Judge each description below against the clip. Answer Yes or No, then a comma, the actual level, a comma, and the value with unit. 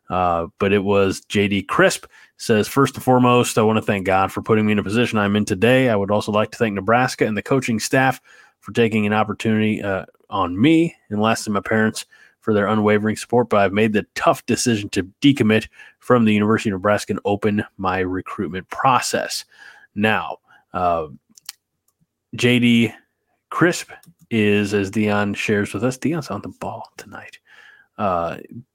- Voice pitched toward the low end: Yes, low, 110 Hz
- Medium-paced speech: Yes, average, 175 wpm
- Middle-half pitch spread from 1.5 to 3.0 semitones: Yes, narrow, 2.4 semitones